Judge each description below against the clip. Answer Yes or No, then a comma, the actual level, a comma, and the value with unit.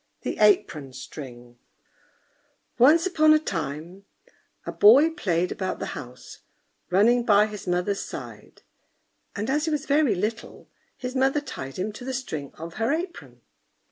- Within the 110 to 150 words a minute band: Yes, average, 145 wpm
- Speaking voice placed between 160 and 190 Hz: No, high, 210 Hz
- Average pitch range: No, wide, 8.2 semitones